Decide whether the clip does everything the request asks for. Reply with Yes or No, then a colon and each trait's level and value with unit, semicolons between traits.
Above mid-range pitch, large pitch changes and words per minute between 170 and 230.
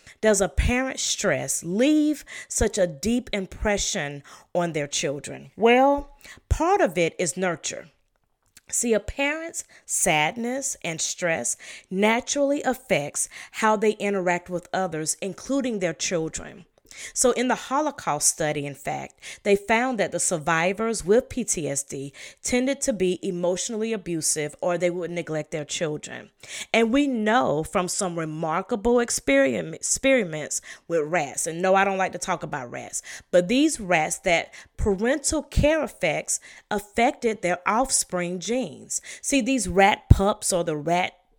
No: high, 195 Hz; wide, 6.3 semitones; average, 140 wpm